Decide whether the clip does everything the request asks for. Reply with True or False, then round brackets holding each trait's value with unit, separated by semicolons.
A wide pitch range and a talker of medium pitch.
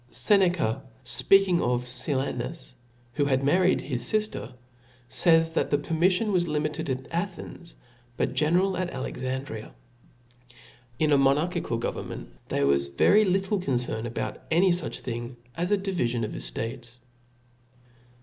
True (6.4 semitones; 150 Hz)